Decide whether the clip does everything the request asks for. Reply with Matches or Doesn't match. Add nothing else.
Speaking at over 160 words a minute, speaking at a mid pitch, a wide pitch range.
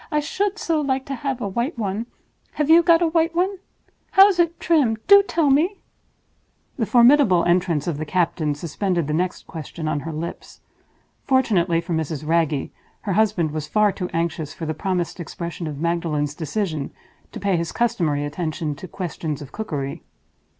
Matches